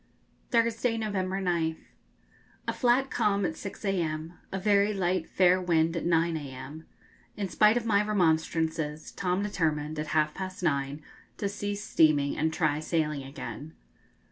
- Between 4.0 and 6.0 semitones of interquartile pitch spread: Yes, average, 4.4 semitones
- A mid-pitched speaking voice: Yes, medium, 175 Hz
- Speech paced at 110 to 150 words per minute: Yes, average, 145 wpm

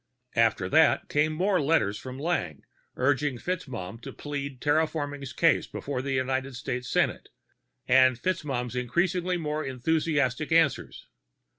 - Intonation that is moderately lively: Yes, average, 3.9 semitones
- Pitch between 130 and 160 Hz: Yes, medium, 140 Hz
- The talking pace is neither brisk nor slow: No, slow, 125 wpm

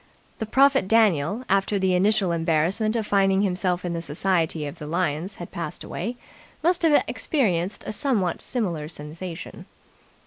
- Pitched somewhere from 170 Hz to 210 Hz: Yes, medium, 185 Hz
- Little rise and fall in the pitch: No, average, 4.3 semitones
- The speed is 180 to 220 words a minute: No, average, 150 wpm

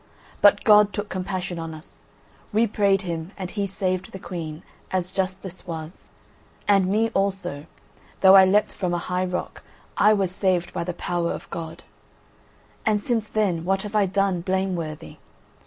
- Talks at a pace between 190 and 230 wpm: No, average, 160 wpm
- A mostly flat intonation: Yes, narrow, 2.3 semitones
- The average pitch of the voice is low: No, high, 190 Hz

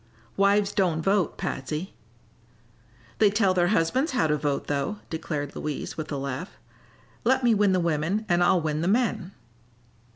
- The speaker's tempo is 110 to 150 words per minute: No, average, 160 wpm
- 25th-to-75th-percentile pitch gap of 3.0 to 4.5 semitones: No, average, 5.1 semitones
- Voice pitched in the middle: Yes, medium, 175 Hz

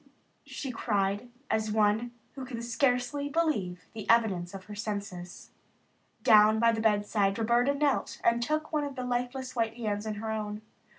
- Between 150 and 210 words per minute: Yes, average, 165 wpm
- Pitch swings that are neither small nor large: Yes, average, 3.2 semitones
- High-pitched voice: Yes, high, 225 Hz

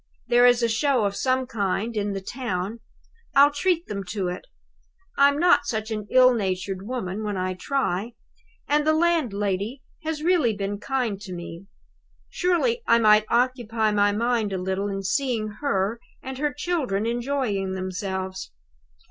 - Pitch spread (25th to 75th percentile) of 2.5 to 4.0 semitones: No, average, 5.2 semitones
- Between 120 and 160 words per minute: Yes, average, 155 wpm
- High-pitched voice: Yes, high, 225 Hz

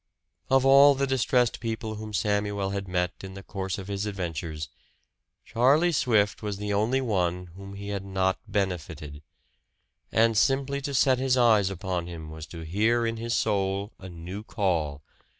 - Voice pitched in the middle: No, low, 100 Hz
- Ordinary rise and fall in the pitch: Yes, average, 3.9 semitones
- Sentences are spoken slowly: No, average, 165 wpm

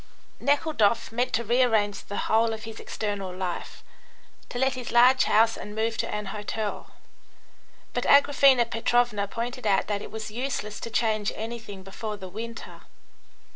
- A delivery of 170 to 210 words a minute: No, average, 155 wpm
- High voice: Yes, high, 225 Hz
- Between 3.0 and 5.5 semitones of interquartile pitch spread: No, narrow, 2.6 semitones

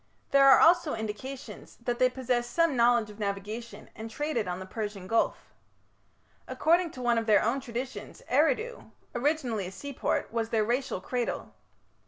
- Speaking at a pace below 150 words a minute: No, average, 160 wpm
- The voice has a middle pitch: No, high, 240 Hz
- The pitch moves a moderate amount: Yes, average, 3.7 semitones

